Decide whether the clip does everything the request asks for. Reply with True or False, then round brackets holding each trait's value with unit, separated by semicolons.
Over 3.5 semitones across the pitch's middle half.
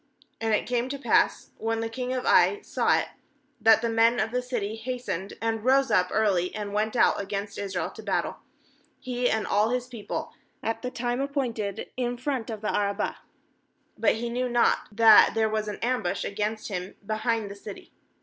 False (2.8 semitones)